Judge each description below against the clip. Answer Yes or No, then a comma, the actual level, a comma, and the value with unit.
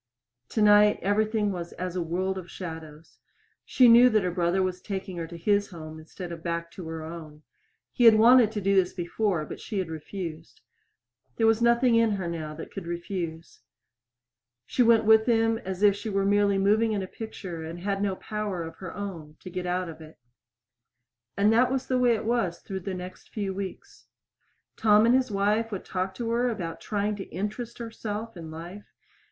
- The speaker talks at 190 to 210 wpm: Yes, average, 200 wpm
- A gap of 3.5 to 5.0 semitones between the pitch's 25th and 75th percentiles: Yes, average, 4.2 semitones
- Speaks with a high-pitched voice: Yes, high, 195 Hz